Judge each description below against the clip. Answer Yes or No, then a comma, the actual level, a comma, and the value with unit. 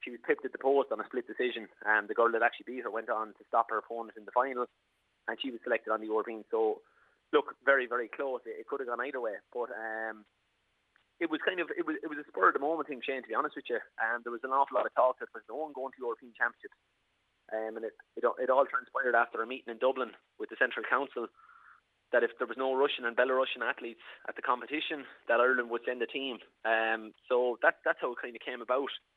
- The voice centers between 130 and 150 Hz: Yes, low, 135 Hz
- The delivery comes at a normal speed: No, fast, 270 wpm